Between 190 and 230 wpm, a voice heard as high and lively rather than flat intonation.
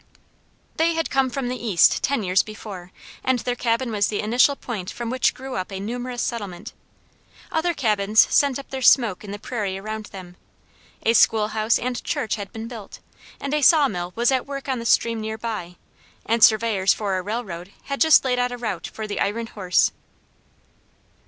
No: average, 195 wpm; high, 225 Hz; average, 3.6 semitones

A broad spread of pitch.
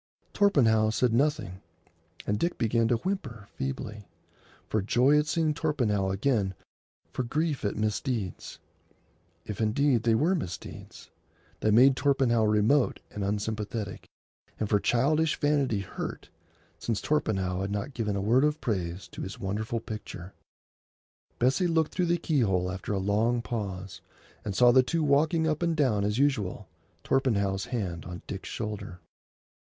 Yes: wide, 5.7 semitones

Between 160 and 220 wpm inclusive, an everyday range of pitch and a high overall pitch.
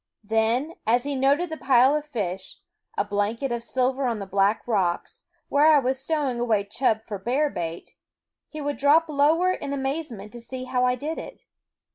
Yes: average, 190 wpm; average, 4.6 semitones; very high, 255 Hz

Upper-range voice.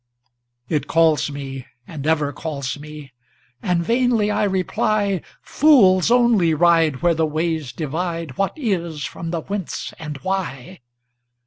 No: medium, 165 Hz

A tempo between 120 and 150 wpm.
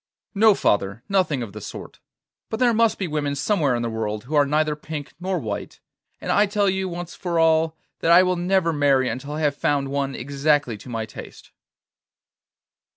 No: average, 195 wpm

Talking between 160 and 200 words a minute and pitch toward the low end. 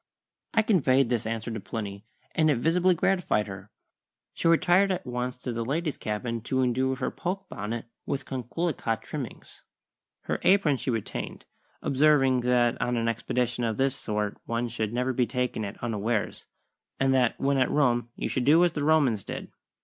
Yes: average, 175 wpm; low, 125 Hz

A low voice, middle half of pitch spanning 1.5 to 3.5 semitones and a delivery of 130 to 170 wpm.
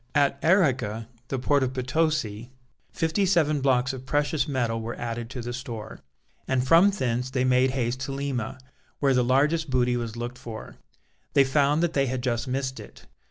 No: low, 130 Hz; average, 2.9 semitones; average, 180 wpm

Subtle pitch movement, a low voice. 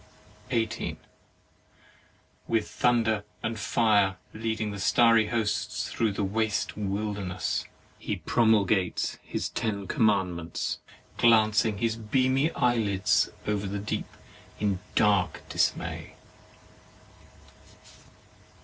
Yes: narrow, 2.2 semitones; low, 105 Hz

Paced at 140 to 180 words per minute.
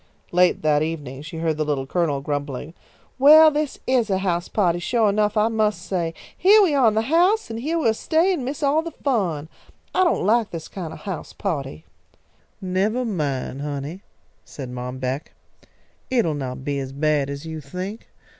No: average, 190 wpm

